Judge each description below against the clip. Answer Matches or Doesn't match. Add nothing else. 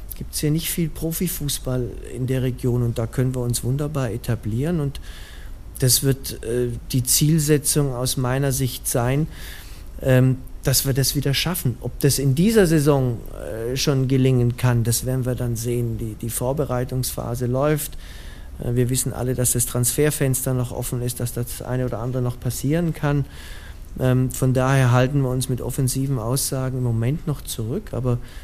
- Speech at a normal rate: Matches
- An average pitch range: Doesn't match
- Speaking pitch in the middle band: Doesn't match